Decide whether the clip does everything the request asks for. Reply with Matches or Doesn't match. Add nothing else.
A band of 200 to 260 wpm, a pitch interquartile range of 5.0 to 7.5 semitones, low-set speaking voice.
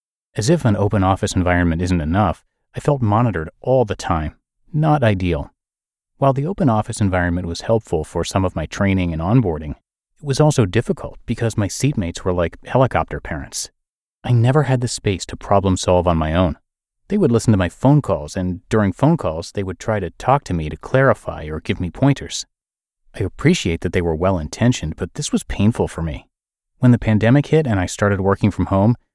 Matches